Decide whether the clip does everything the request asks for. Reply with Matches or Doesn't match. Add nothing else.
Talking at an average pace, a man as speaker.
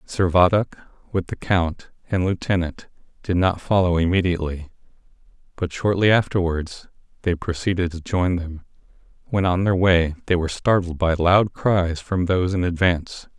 Matches